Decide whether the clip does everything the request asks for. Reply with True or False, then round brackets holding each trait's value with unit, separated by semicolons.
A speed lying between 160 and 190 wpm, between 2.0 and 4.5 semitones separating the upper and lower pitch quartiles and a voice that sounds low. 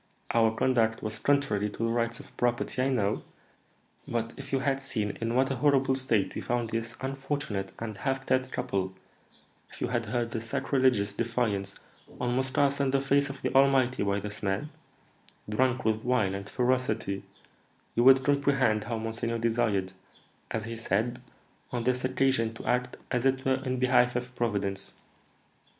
True (170 wpm; 3.1 semitones; 120 Hz)